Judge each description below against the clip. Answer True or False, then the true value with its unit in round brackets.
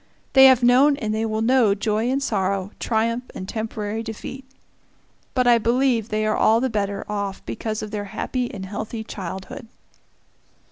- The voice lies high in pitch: True (220 Hz)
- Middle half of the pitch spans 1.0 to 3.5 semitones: True (2.8 semitones)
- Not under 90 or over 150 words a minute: False (170 wpm)